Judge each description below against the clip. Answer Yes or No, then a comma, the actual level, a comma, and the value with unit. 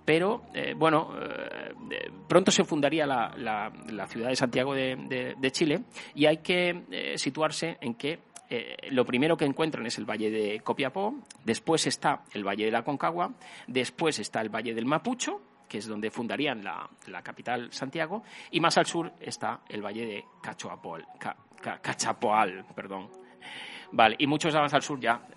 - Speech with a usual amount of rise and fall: No, wide, 6.3 semitones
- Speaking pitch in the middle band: Yes, medium, 145 Hz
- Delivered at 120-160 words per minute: No, average, 175 wpm